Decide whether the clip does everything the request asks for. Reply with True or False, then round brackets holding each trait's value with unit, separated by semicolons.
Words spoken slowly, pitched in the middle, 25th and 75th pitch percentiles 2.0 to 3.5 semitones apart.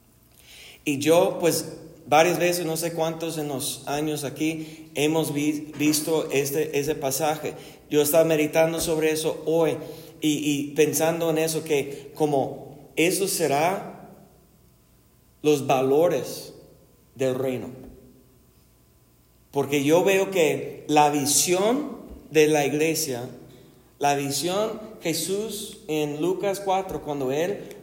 True (115 wpm; 155 Hz; 2.5 semitones)